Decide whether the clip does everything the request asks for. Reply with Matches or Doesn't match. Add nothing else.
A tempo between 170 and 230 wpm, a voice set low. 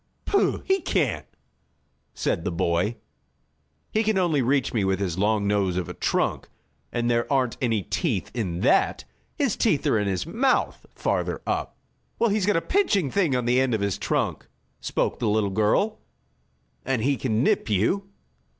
Matches